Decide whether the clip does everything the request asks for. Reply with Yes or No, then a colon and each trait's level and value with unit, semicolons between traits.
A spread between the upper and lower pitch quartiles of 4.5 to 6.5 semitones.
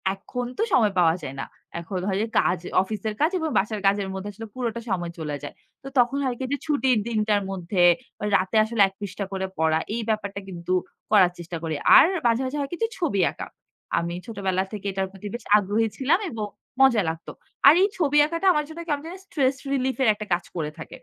Yes: wide, 5.5 semitones